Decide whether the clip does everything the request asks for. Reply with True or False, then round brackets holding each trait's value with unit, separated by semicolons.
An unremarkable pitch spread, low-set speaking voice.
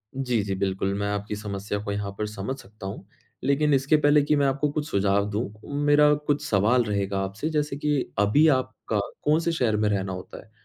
False (6.4 semitones; 110 Hz)